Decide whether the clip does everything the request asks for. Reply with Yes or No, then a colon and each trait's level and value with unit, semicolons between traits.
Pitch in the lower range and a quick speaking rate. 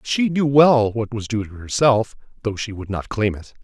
Yes: low, 115 Hz; fast, 230 wpm